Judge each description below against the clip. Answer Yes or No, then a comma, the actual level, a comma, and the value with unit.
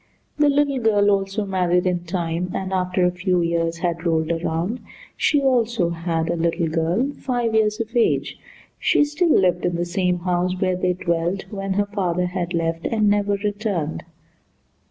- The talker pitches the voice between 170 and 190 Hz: Yes, medium, 185 Hz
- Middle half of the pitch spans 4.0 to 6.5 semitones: No, average, 3.4 semitones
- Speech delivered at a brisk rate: No, average, 175 wpm